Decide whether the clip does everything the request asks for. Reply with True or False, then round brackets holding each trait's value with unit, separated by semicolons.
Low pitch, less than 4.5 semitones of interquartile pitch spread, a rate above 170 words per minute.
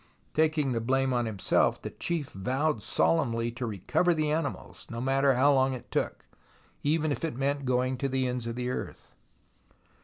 True (130 Hz; 3.2 semitones; 180 wpm)